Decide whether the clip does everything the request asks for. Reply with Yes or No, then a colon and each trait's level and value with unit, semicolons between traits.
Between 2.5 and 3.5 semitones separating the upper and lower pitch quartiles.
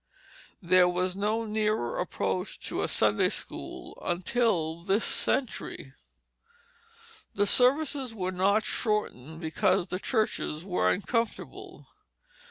No: average, 4.1 semitones